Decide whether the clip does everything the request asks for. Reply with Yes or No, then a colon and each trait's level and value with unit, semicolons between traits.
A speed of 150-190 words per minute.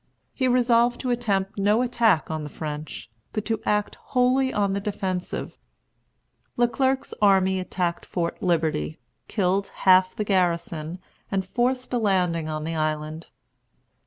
No: average, 140 wpm